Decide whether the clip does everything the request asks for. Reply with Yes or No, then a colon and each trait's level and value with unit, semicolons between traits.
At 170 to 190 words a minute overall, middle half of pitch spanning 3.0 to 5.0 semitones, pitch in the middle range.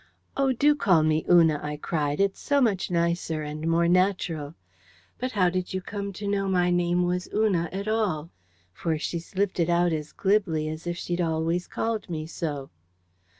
Yes: average, 185 wpm; average, 3.6 semitones; medium, 175 Hz